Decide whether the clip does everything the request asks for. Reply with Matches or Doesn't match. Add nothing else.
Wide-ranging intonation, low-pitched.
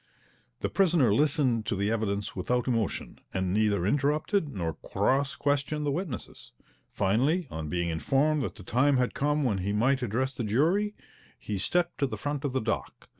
Matches